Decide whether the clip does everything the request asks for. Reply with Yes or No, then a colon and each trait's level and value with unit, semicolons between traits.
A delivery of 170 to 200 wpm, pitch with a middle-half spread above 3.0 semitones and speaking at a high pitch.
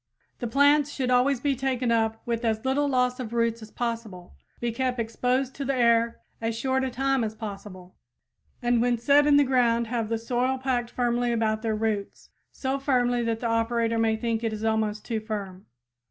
No: average, 195 wpm; narrow, 2.4 semitones; high, 235 Hz